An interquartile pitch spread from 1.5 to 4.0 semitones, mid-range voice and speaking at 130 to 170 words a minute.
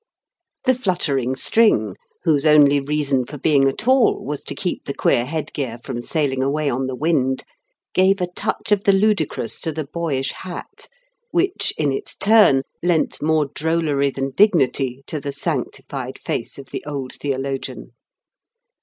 No: average, 4.5 semitones; medium, 145 Hz; average, 160 wpm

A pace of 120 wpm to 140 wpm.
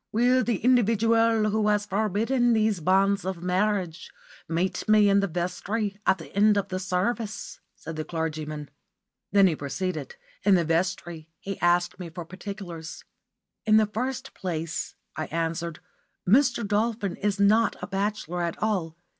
No: average, 155 wpm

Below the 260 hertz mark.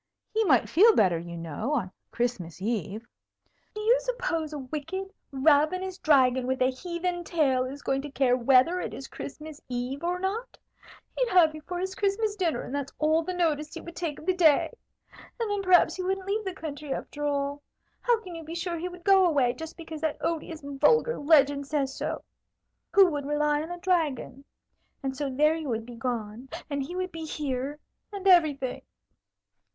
No: very high, 305 Hz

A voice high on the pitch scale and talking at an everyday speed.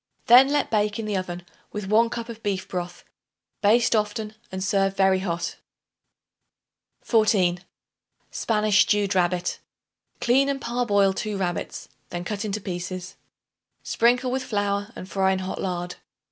Yes: high, 205 Hz; average, 145 wpm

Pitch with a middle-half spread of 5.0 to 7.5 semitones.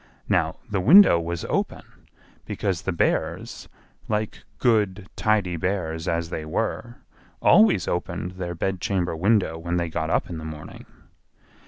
No: average, 3.3 semitones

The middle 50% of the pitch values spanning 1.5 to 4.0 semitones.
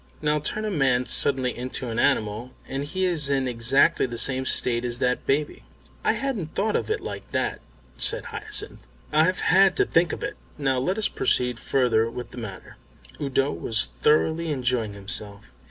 No: average, 4.9 semitones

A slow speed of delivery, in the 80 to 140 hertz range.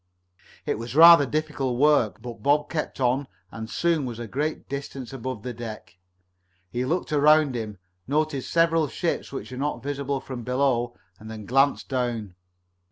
No: average, 165 wpm; low, 135 Hz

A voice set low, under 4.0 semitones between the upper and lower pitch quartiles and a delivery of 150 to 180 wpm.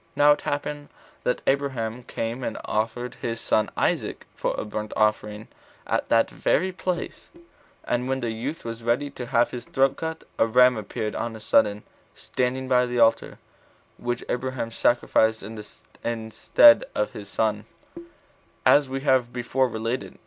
Yes: low, 120 Hz; average, 2.8 semitones; average, 160 wpm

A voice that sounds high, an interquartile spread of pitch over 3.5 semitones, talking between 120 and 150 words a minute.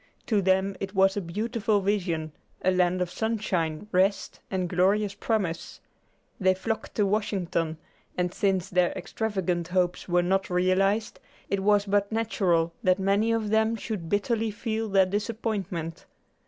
No: high, 195 Hz; average, 2.7 semitones; average, 145 wpm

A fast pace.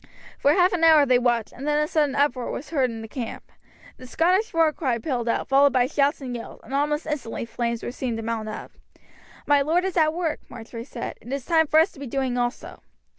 Yes: fast, 235 wpm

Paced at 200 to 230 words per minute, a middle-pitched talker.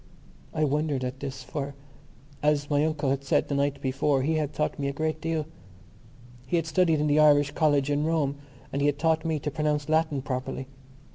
Yes: fast, 205 wpm; medium, 145 Hz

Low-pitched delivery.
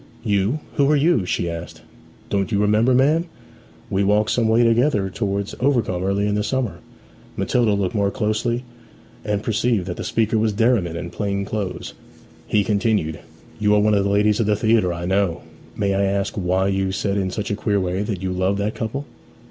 Yes: low, 105 Hz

